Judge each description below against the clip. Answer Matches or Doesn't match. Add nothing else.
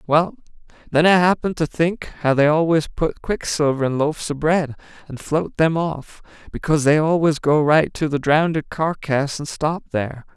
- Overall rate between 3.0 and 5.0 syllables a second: Matches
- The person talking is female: Doesn't match